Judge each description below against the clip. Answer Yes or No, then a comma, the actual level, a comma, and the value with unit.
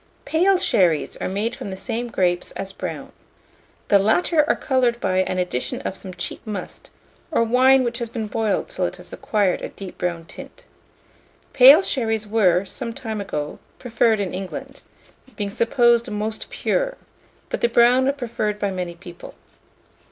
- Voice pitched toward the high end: Yes, high, 220 Hz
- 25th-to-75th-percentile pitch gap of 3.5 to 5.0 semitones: Yes, average, 4.2 semitones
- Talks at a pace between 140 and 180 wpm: Yes, average, 165 wpm